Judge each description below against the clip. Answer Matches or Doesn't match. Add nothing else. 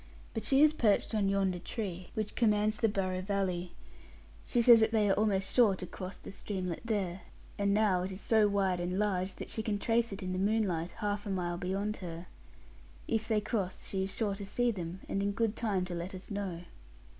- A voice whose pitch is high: Matches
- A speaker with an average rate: Doesn't match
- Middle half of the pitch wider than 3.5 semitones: Doesn't match